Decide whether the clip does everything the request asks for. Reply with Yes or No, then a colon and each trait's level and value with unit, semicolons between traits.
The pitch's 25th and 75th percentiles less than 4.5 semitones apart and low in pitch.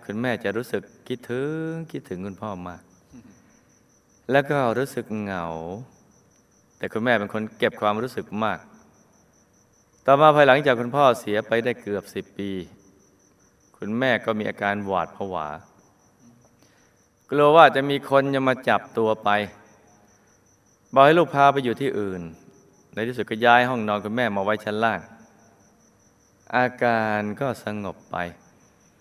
Yes: average, 4.1 semitones; low, 110 Hz